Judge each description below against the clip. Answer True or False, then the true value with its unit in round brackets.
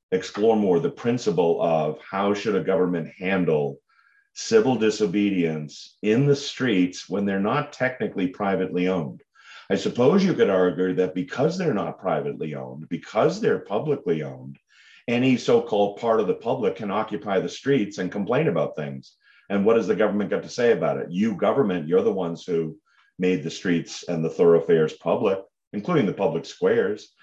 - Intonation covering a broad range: True (6.4 semitones)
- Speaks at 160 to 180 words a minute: True (170 wpm)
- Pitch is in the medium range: False (100 Hz)